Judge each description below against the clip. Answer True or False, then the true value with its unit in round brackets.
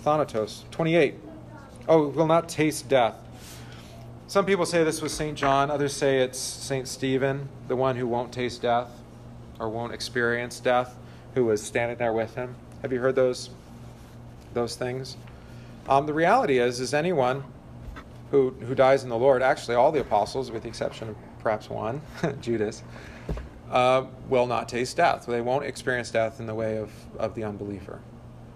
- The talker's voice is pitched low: True (125 Hz)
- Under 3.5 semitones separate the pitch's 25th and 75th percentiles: True (2.8 semitones)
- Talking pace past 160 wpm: True (170 wpm)